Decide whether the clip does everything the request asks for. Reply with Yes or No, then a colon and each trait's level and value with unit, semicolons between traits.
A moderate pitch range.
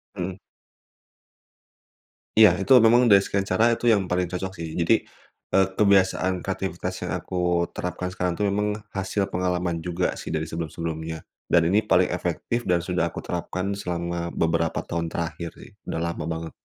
No: narrow, 2.3 semitones